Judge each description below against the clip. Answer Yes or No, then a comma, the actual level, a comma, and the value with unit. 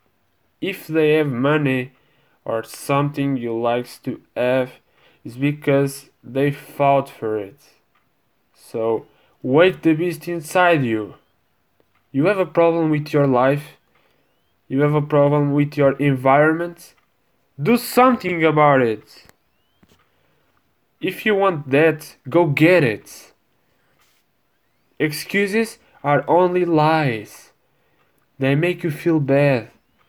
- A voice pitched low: No, medium, 145 Hz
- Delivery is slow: Yes, slow, 110 wpm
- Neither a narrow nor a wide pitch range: Yes, average, 3.5 semitones